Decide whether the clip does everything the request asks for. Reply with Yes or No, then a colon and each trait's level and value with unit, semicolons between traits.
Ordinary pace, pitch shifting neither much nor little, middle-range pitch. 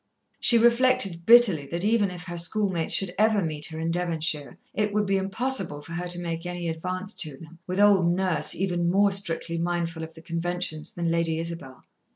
Yes: average, 195 wpm; average, 3.0 semitones; medium, 175 Hz